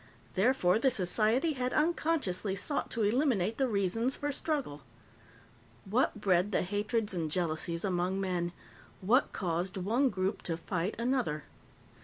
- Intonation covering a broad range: Yes, wide, 5.8 semitones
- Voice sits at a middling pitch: No, high, 205 Hz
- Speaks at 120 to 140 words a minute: Yes, slow, 135 wpm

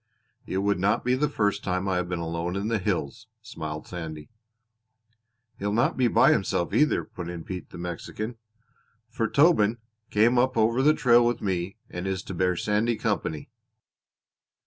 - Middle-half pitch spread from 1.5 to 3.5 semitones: No, average, 4.7 semitones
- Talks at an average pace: Yes, average, 170 wpm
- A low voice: Yes, low, 100 Hz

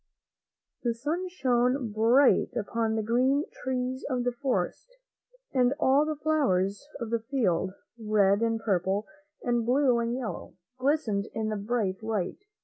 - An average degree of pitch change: Yes, average, 3.6 semitones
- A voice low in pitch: No, high, 235 Hz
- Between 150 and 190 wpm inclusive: No, average, 140 wpm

